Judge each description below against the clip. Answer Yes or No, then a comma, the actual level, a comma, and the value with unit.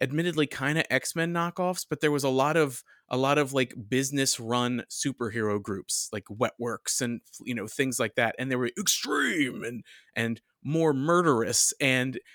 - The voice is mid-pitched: No, low, 130 Hz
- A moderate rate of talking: Yes, average, 175 wpm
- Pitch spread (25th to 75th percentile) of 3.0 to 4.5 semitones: Yes, average, 3.7 semitones